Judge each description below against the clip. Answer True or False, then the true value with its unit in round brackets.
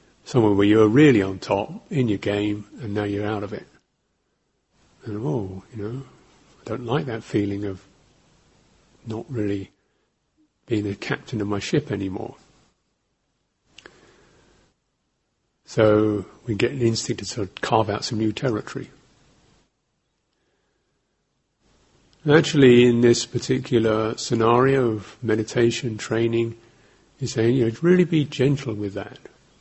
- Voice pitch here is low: True (115 Hz)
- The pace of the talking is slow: True (130 wpm)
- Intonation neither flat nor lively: True (3.4 semitones)